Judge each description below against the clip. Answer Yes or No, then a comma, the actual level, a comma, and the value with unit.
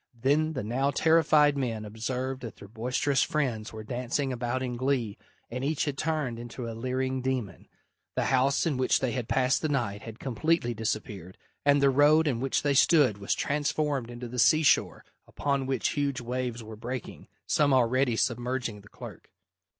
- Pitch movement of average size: Yes, average, 3.1 semitones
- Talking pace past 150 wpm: Yes, average, 180 wpm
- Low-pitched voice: Yes, low, 130 Hz